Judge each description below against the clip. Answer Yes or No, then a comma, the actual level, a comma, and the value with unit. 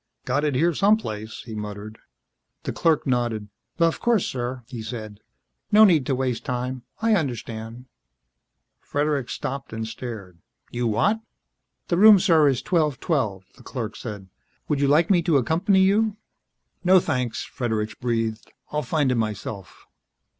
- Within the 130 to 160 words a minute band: Yes, average, 155 wpm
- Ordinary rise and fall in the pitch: No, wide, 6.5 semitones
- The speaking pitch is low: Yes, low, 130 Hz